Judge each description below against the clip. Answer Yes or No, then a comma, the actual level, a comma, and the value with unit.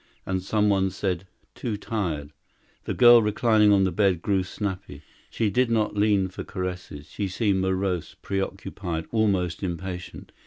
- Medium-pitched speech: No, very low, 95 Hz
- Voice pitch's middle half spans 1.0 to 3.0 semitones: Yes, narrow, 2.5 semitones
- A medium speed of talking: Yes, average, 150 wpm